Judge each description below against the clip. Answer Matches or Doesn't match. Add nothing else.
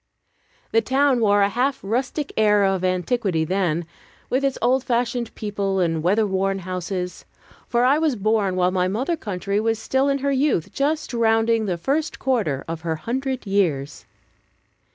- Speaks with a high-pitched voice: Matches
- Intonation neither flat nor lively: Doesn't match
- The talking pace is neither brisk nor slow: Matches